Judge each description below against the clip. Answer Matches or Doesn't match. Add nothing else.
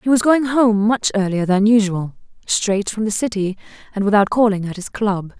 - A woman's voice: Matches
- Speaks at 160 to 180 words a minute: Doesn't match